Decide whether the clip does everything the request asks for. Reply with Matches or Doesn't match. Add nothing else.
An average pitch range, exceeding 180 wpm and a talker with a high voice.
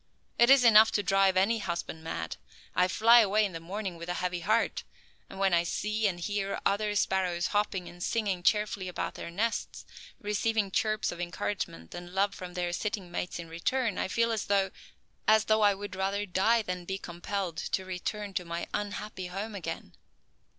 Matches